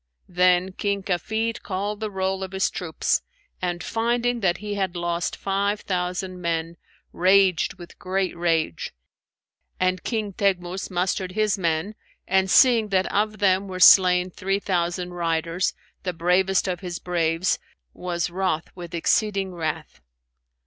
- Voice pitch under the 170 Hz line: No, medium, 185 Hz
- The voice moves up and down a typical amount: No, narrow, 2.0 semitones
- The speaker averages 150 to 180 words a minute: No, average, 140 wpm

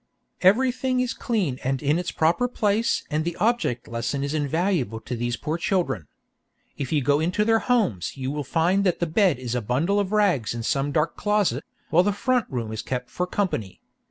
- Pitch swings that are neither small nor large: No, wide, 7.9 semitones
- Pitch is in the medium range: Yes, medium, 160 Hz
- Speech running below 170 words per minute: No, average, 200 wpm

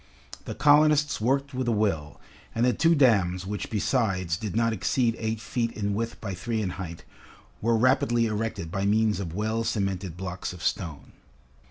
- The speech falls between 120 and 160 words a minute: No, average, 175 wpm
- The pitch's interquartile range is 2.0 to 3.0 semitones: No, average, 3.8 semitones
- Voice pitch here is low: Yes, low, 110 Hz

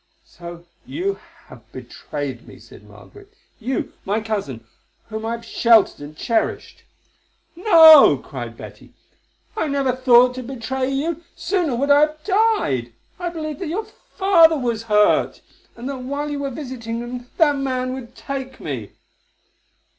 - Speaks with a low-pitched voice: No, very high, 260 Hz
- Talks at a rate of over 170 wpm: No, average, 145 wpm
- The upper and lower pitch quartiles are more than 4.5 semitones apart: Yes, average, 5.3 semitones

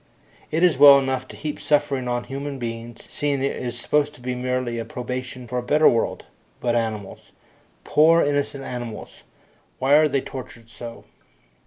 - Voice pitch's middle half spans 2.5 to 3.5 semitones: Yes, average, 3.0 semitones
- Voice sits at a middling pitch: No, low, 130 Hz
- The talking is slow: No, average, 170 wpm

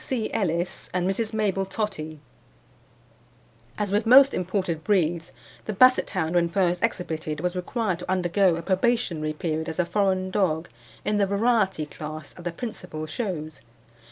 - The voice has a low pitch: No, medium, 185 Hz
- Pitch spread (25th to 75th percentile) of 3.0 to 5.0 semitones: Yes, average, 4.1 semitones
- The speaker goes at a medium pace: Yes, average, 155 wpm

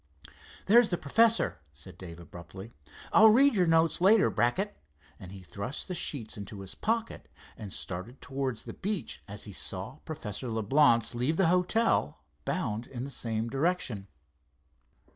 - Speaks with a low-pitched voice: Yes, low, 130 Hz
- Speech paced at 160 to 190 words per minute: No, average, 150 wpm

